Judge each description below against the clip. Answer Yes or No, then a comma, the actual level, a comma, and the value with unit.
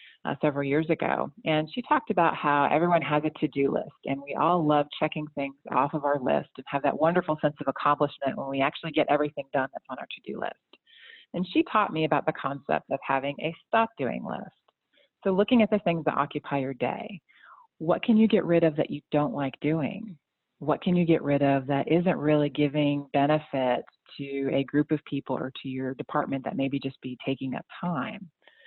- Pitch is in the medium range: Yes, medium, 150 Hz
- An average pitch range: Yes, average, 3.0 semitones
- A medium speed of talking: No, fast, 220 wpm